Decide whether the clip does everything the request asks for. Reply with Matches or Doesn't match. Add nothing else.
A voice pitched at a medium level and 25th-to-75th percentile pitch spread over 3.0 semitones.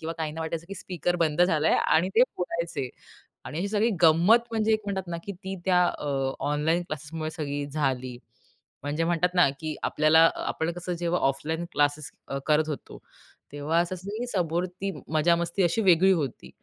Doesn't match